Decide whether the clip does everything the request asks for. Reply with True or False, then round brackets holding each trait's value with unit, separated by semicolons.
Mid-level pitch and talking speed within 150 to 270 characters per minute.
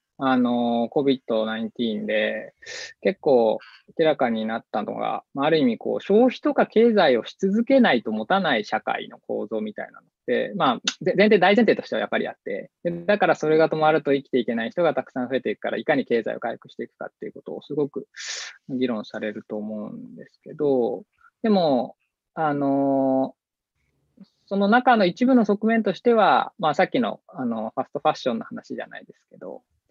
False (155 Hz; 355 characters per minute)